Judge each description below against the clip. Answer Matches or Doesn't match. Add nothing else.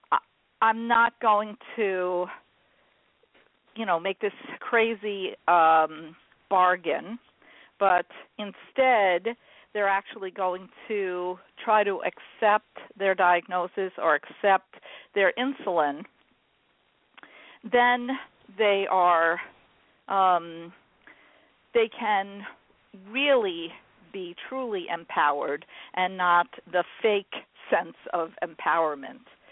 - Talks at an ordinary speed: Doesn't match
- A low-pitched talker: Doesn't match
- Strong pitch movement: Doesn't match